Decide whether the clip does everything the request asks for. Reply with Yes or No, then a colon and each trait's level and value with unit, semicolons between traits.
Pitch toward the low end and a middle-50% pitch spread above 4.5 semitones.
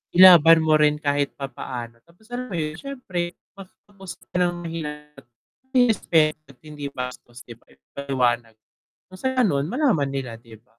No: medium, 150 Hz; average, 4.9 semitones